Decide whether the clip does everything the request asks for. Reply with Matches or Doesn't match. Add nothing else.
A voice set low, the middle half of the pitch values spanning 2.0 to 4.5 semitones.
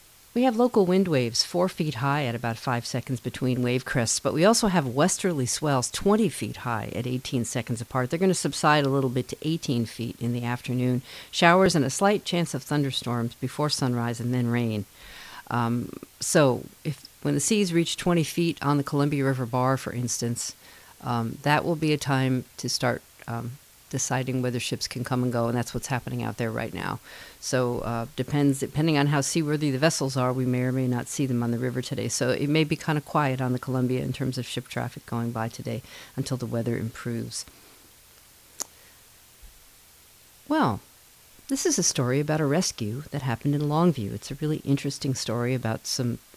Matches